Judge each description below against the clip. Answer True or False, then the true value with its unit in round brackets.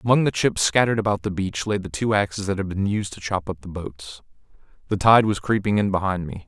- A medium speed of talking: False (250 wpm)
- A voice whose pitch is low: True (100 Hz)